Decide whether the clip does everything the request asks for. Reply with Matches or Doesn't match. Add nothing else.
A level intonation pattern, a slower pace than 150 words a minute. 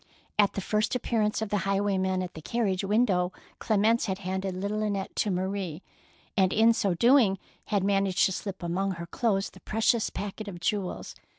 Doesn't match